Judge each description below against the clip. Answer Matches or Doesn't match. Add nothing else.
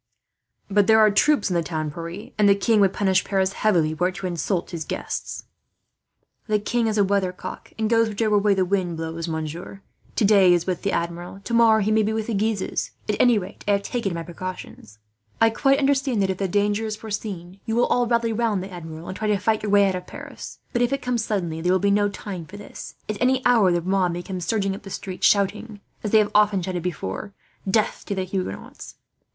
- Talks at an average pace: Doesn't match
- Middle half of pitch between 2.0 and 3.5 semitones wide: Matches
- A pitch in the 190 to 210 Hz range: Matches